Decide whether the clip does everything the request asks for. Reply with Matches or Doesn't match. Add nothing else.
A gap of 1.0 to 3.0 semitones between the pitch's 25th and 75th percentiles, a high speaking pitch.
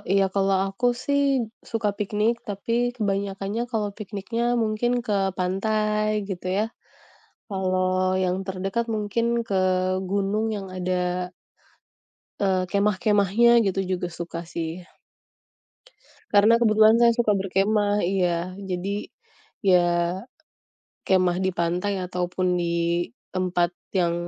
Matches